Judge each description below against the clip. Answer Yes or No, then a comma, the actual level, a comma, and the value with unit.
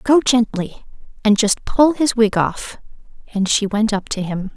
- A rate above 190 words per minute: No, average, 185 wpm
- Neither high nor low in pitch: No, high, 220 Hz